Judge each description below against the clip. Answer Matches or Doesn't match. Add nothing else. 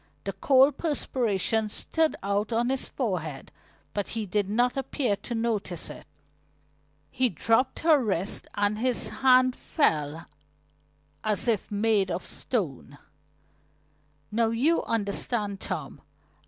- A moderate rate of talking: Doesn't match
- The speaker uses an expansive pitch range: Doesn't match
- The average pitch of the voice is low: Doesn't match